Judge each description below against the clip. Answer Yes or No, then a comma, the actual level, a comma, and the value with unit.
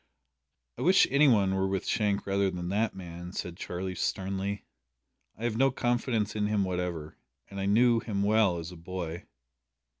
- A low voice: Yes, low, 100 Hz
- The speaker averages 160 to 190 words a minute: Yes, average, 175 wpm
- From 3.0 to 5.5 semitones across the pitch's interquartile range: Yes, average, 3.3 semitones